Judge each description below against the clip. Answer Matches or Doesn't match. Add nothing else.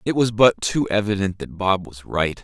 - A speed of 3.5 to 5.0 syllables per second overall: Matches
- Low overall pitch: Matches